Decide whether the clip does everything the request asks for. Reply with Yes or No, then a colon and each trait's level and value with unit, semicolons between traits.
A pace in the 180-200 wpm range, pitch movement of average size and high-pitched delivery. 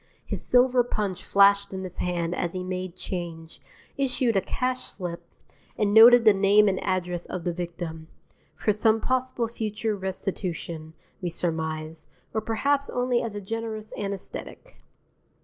No: average, 150 wpm; average, 4.3 semitones; high, 195 Hz